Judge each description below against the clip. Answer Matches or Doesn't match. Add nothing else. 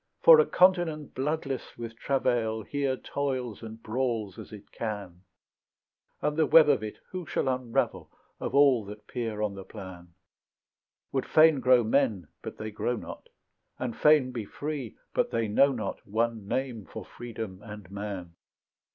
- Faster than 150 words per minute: Matches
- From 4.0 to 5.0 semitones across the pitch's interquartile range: Matches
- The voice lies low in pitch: Matches